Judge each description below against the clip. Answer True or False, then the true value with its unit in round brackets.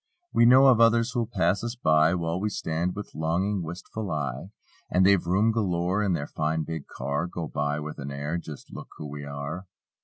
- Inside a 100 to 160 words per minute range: False (205 wpm)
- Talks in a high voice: False (85 Hz)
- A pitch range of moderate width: True (4.9 semitones)